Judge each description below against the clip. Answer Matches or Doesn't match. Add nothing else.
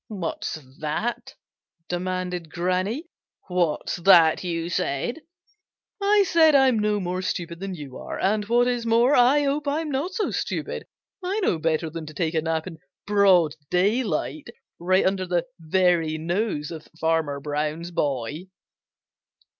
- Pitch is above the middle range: Doesn't match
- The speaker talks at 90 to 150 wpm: Matches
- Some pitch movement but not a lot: Doesn't match